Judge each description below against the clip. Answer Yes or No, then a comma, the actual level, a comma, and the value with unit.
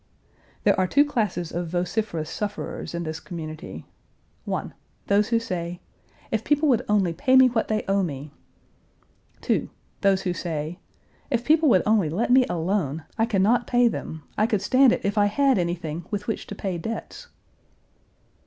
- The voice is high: Yes, high, 200 Hz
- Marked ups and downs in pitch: No, average, 5.0 semitones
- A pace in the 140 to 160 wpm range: No, average, 170 wpm